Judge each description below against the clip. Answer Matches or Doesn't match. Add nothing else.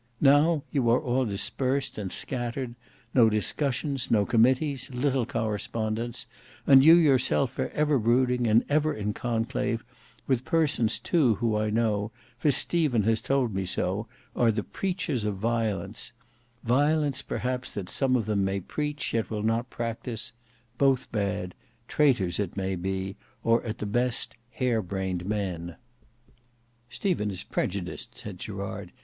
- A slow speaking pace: Doesn't match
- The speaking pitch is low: Matches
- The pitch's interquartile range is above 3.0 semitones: Matches